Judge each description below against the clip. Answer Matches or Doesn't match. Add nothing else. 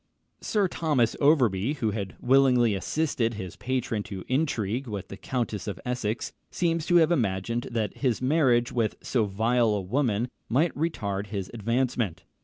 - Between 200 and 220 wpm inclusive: Doesn't match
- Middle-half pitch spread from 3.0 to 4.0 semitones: Doesn't match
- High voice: Doesn't match